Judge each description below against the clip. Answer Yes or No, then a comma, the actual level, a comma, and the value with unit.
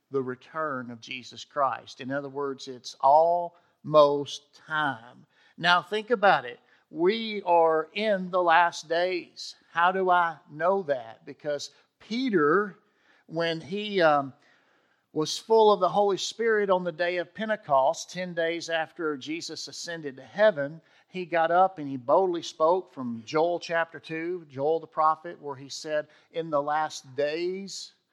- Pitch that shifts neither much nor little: Yes, average, 4.0 semitones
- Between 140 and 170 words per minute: Yes, average, 150 wpm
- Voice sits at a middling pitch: Yes, medium, 165 Hz